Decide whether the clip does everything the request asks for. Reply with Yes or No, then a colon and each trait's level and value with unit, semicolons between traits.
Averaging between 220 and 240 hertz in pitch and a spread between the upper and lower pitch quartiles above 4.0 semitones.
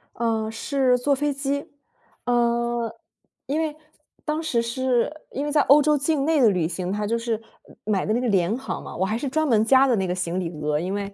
Yes: high, 235 Hz; average, 5.1 semitones